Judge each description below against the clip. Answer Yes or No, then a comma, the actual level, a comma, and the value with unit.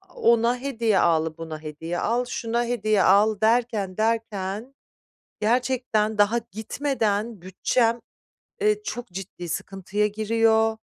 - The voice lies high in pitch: Yes, high, 220 Hz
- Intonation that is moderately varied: Yes, average, 3.4 semitones